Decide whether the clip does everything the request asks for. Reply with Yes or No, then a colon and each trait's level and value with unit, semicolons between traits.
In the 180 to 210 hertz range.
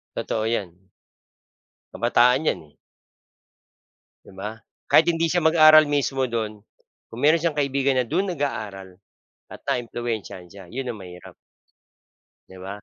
No: low, 120 Hz